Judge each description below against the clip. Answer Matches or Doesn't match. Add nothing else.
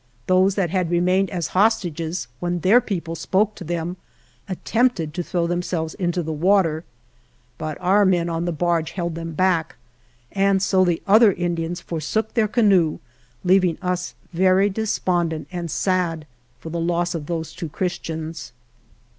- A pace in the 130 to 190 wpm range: Matches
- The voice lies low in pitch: Doesn't match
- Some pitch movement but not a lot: Doesn't match